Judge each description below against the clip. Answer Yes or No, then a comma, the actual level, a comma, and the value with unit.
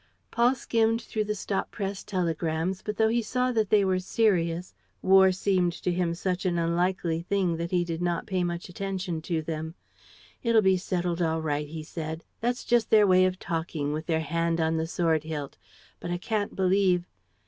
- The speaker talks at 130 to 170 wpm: No, average, 190 wpm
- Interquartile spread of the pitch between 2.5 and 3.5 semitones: Yes, average, 3.1 semitones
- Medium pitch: Yes, medium, 180 Hz